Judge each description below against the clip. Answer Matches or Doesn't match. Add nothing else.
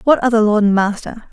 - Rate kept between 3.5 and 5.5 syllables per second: Doesn't match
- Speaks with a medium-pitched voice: Doesn't match